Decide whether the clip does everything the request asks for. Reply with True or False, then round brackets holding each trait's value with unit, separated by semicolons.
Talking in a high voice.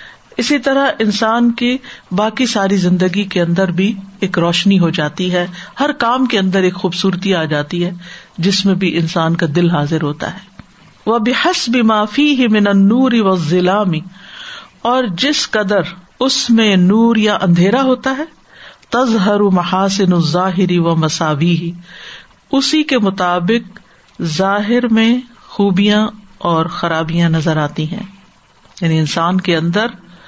True (195 Hz)